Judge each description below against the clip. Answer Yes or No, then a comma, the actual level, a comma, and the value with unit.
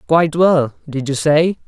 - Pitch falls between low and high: Yes, medium, 150 Hz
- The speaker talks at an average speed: Yes, average, 180 wpm